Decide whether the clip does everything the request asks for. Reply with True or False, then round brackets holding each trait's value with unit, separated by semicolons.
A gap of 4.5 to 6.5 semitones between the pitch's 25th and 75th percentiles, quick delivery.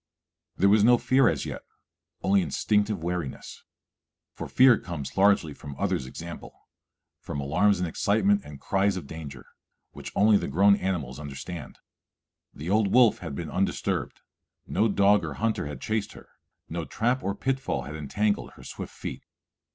False (5.2 semitones; 160 wpm)